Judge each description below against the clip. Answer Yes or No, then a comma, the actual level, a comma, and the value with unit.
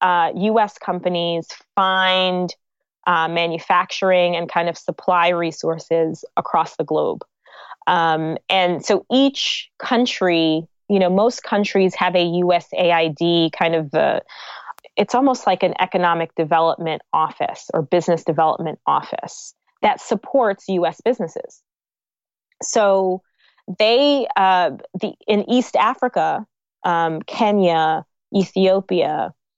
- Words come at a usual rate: No, slow, 110 wpm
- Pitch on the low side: No, medium, 180 Hz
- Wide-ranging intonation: No, average, 3.5 semitones